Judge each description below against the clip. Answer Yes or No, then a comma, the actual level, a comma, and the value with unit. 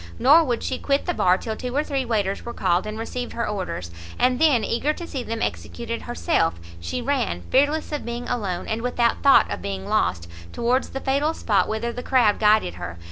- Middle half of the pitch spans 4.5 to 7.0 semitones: Yes, average, 5.1 semitones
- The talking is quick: Yes, fast, 210 wpm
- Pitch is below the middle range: No, high, 235 Hz